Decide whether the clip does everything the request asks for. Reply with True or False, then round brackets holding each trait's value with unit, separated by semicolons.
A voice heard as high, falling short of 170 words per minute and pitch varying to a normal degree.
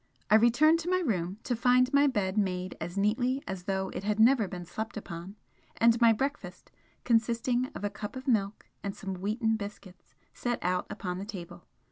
False (215 Hz; 190 wpm; 4.2 semitones)